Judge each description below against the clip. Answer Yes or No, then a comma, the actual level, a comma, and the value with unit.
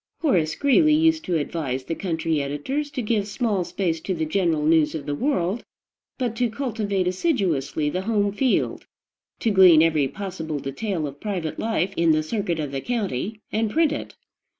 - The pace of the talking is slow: No, average, 175 wpm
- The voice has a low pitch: No, medium, 185 Hz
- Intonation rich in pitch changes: Yes, wide, 6.1 semitones